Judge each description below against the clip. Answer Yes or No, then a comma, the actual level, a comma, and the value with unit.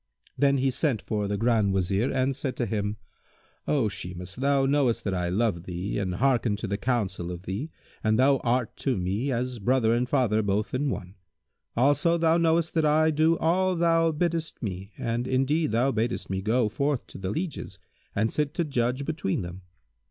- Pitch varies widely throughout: Yes, wide, 5.9 semitones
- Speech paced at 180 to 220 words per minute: Yes, average, 190 wpm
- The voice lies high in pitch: No, low, 125 Hz